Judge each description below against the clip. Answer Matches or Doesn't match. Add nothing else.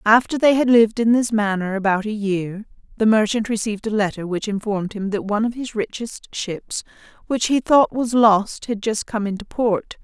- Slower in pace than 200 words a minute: Doesn't match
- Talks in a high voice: Matches